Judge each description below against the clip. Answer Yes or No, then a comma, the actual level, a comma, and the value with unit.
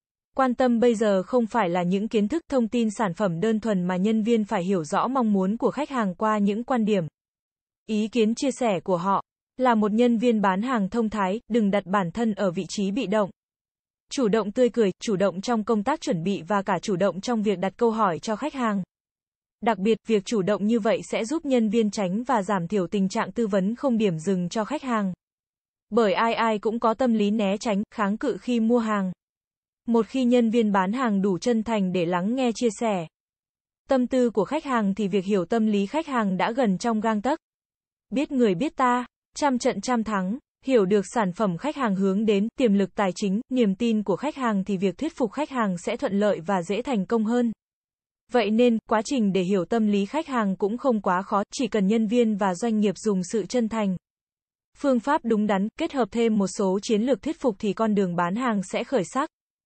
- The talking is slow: No, average, 235 wpm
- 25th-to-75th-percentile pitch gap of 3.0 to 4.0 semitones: Yes, average, 3.3 semitones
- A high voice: Yes, high, 220 Hz